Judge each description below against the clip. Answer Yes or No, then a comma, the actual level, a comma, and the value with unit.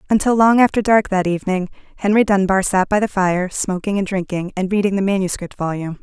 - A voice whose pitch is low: No, high, 195 Hz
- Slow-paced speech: No, average, 200 wpm